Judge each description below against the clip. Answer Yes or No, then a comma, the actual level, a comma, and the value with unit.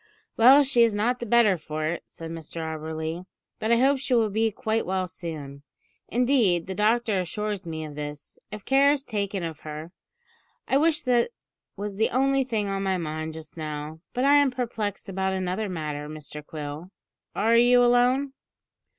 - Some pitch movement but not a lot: No, wide, 7.1 semitones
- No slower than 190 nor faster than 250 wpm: No, average, 180 wpm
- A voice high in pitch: Yes, high, 195 Hz